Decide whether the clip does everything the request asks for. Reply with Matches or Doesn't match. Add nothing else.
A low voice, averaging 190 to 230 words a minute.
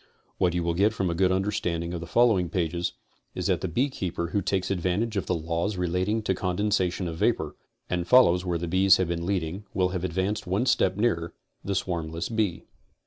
Matches